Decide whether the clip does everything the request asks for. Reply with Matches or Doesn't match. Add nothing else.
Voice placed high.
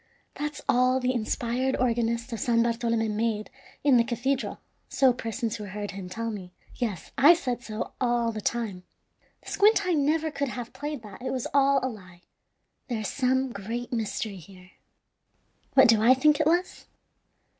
Matches